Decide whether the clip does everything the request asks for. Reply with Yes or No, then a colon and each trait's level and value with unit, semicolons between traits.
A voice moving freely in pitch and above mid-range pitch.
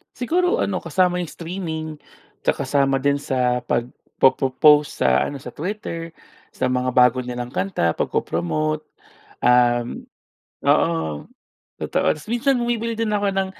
No: wide, 7.8 semitones; medium, 145 Hz